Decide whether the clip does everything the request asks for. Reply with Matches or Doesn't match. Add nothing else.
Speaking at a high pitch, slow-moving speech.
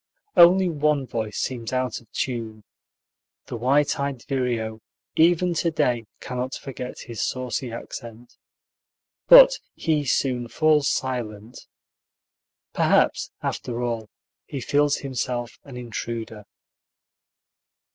Doesn't match